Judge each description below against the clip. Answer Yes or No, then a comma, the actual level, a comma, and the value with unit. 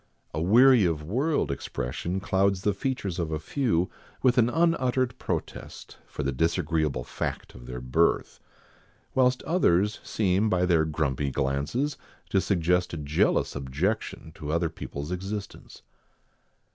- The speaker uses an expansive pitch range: Yes, wide, 6.3 semitones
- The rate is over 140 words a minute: No, slow, 135 wpm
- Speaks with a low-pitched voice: Yes, very low, 90 Hz